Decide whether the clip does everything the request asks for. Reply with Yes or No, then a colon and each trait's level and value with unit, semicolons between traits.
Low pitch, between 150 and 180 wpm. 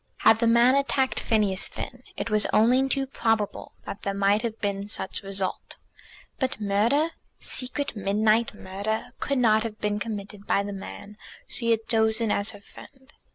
No: high, 220 Hz; average, 165 wpm